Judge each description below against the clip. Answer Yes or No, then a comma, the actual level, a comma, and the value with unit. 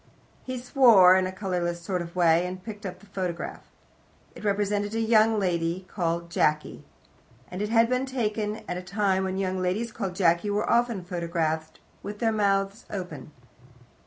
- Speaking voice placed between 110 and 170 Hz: No, high, 190 Hz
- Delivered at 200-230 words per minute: No, average, 165 wpm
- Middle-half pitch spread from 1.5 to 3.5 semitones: Yes, average, 3.1 semitones